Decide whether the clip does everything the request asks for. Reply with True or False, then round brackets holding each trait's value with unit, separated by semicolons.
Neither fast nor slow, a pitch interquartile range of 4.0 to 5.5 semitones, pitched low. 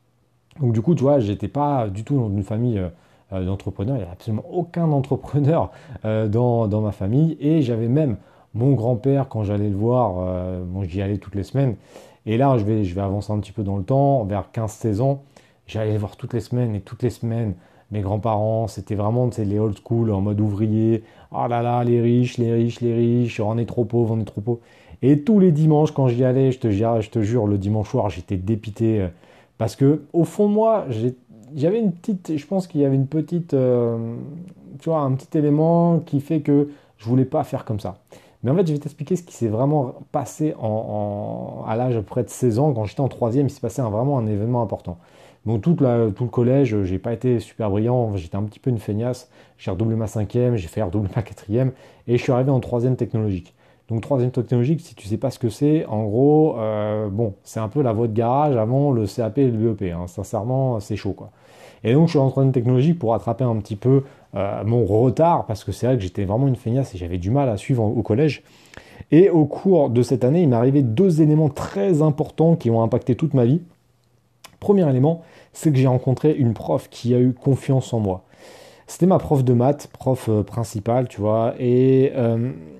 False (235 wpm; 4.3 semitones; 120 Hz)